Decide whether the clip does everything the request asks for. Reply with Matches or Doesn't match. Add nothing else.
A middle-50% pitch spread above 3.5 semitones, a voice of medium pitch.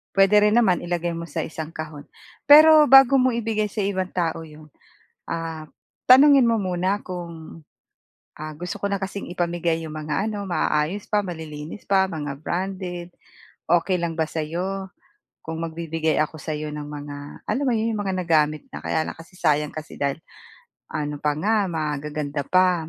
Matches